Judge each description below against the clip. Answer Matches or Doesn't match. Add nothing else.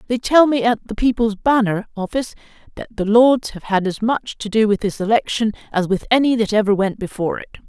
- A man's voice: Doesn't match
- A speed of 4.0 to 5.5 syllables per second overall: Doesn't match